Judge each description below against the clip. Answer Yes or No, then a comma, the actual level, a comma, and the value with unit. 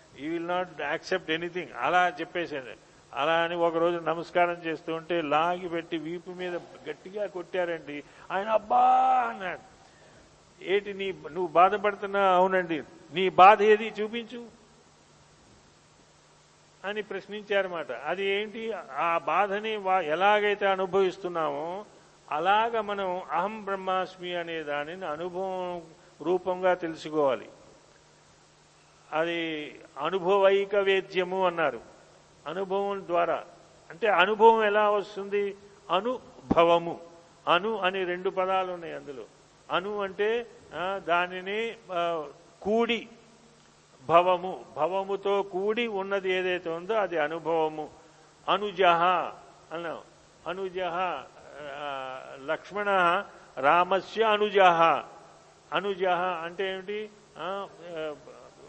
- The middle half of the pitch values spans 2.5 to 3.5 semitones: Yes, average, 3.1 semitones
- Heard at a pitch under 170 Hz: No, medium, 180 Hz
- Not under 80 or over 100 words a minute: Yes, average, 85 wpm